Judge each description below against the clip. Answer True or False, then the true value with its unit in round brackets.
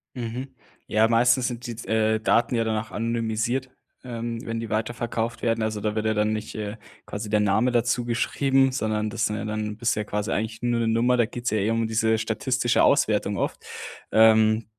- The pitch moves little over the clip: True (1.7 semitones)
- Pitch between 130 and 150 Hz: False (115 Hz)